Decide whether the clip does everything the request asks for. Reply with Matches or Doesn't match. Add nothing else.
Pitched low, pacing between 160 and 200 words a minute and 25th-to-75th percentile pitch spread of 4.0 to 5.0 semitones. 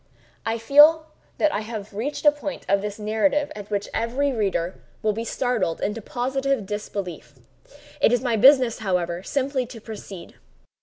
Doesn't match